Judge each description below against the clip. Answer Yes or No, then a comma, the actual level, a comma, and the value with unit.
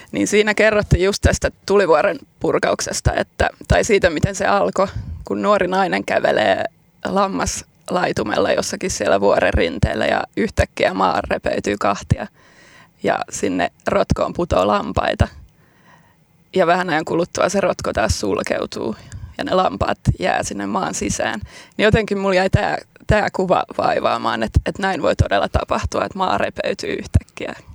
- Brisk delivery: No, average, 140 wpm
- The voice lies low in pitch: No, high, 195 Hz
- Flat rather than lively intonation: Yes, narrow, 2.3 semitones